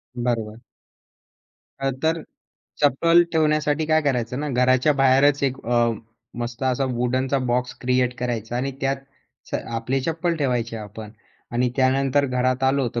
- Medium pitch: No, low, 130 Hz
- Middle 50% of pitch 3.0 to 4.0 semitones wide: No, narrow, 2.5 semitones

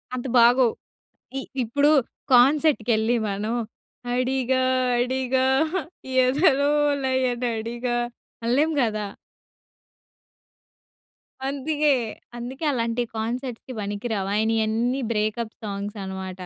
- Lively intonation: No, average, 3.0 semitones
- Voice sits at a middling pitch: No, high, 240 Hz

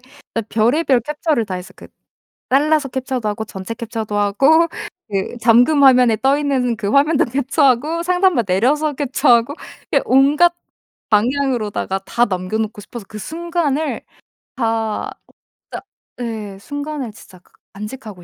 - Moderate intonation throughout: Yes, average, 5.0 semitones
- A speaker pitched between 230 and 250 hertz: Yes, high, 245 Hz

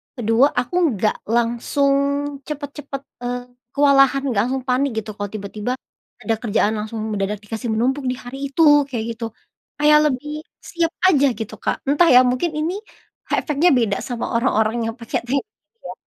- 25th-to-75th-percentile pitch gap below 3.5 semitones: No, average, 4.2 semitones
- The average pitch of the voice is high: Yes, very high, 250 Hz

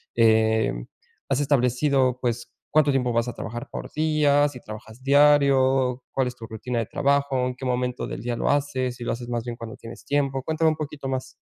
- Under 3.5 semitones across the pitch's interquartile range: Yes, average, 2.8 semitones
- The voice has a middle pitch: No, low, 130 Hz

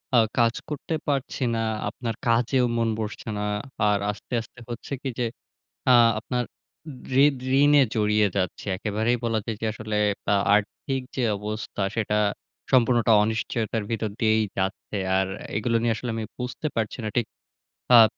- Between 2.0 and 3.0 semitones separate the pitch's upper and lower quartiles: Yes, narrow, 2.4 semitones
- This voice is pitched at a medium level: No, low, 115 Hz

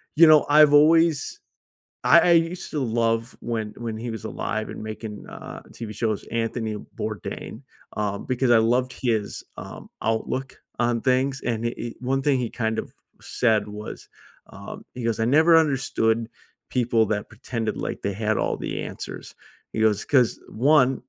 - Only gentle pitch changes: No, average, 3.2 semitones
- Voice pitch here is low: Yes, low, 120 Hz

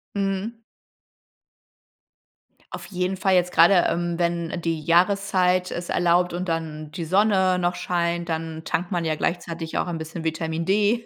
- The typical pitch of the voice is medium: Yes, medium, 175 Hz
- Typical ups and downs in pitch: No, narrow, 2.0 semitones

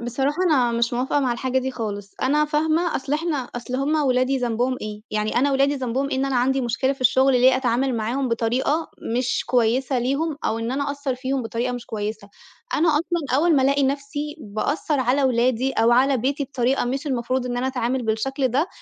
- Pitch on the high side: Yes, very high, 260 Hz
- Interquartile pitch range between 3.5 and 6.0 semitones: No, narrow, 2.6 semitones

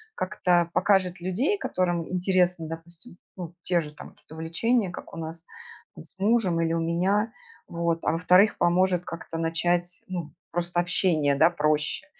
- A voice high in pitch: No, medium, 175 Hz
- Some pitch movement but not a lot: No, narrow, 2.0 semitones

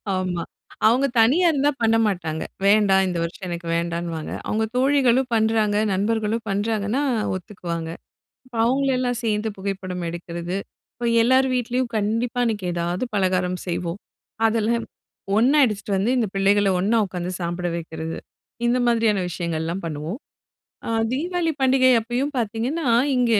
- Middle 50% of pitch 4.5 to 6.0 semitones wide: Yes, average, 5.1 semitones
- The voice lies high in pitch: Yes, high, 210 Hz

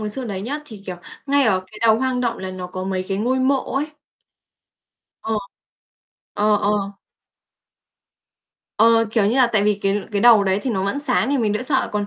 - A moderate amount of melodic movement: Yes, average, 4.3 semitones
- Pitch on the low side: No, high, 220 Hz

